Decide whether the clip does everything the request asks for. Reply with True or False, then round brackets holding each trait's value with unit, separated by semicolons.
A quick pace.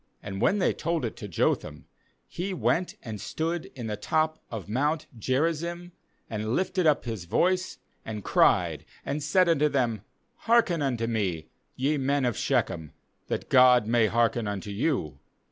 False (160 wpm)